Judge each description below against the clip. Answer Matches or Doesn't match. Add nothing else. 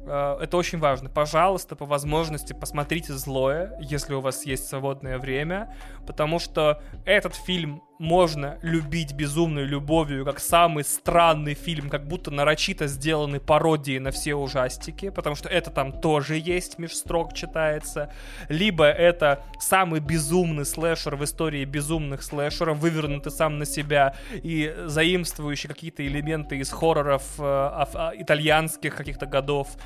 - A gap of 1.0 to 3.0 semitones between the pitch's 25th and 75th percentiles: Matches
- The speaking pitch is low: Doesn't match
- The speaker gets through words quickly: Doesn't match